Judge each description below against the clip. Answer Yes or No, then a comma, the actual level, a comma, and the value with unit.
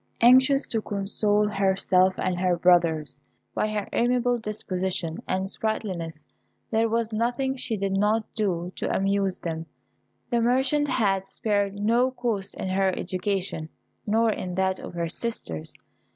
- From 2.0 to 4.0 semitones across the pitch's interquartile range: Yes, average, 3.6 semitones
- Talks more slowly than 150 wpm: Yes, average, 140 wpm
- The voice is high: Yes, high, 200 Hz